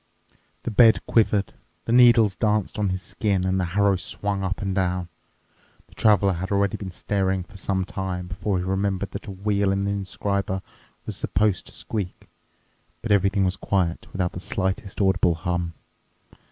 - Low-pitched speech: Yes, very low, 95 Hz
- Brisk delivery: No, average, 170 wpm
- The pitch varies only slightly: Yes, narrow, 1.6 semitones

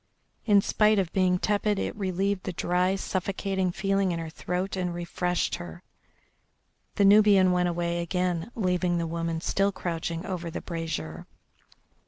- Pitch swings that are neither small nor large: No, narrow, 2.2 semitones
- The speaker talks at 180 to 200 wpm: No, average, 150 wpm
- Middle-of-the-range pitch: Yes, medium, 180 Hz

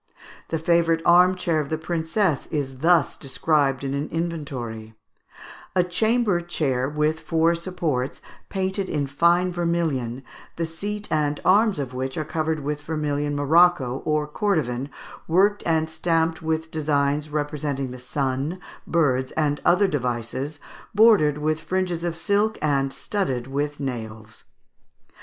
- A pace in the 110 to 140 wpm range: Yes, slow, 135 wpm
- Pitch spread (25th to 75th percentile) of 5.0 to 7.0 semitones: No, average, 3.7 semitones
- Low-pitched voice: No, medium, 155 Hz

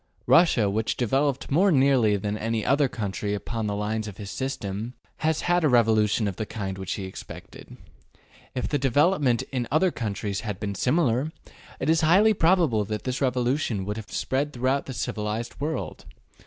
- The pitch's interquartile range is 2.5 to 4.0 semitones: No, wide, 5.4 semitones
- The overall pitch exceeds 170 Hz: No, low, 120 Hz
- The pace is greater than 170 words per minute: Yes, average, 180 wpm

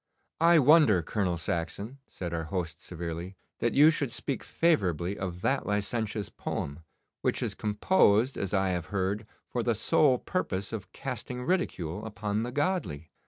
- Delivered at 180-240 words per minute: No, average, 155 wpm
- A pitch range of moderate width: No, wide, 6.0 semitones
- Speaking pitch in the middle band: No, low, 105 Hz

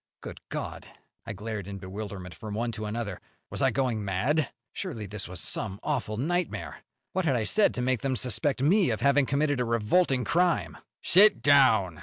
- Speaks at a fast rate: No, average, 185 wpm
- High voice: No, low, 120 Hz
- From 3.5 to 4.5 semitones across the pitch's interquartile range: No, wide, 5.4 semitones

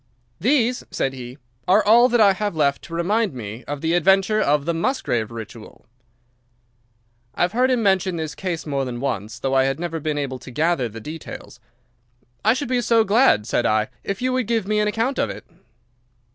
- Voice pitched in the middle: Yes, medium, 170 Hz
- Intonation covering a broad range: Yes, wide, 8.4 semitones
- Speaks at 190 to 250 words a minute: Yes, average, 200 wpm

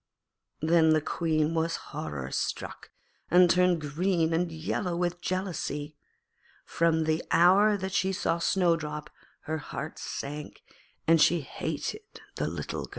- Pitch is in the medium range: Yes, medium, 165 Hz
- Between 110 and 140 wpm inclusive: Yes, slow, 135 wpm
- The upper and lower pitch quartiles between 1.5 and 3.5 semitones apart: Yes, narrow, 2.4 semitones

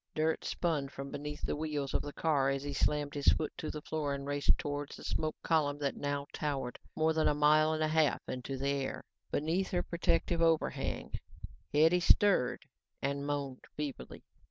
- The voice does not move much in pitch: Yes, narrow, 1.9 semitones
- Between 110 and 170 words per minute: No, average, 185 wpm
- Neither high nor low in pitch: Yes, medium, 145 Hz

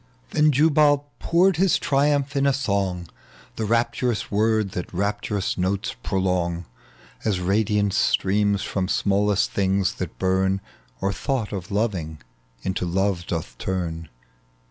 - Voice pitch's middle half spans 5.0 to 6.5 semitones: No, average, 4.0 semitones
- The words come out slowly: Yes, slow, 130 wpm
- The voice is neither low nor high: No, low, 100 Hz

